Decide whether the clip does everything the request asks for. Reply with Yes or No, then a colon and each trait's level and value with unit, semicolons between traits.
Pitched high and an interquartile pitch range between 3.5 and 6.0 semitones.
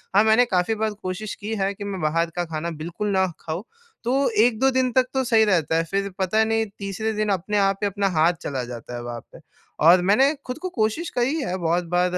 Yes: high, 200 Hz; average, 4.0 semitones